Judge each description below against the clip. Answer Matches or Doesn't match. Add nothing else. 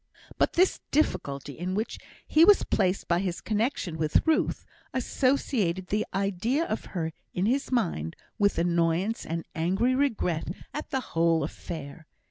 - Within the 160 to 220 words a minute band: Doesn't match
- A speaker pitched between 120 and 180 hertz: Doesn't match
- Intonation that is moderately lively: Doesn't match